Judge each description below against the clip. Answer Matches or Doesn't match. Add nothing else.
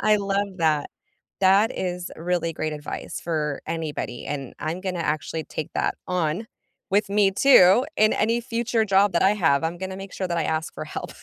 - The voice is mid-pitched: Matches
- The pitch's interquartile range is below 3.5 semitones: Doesn't match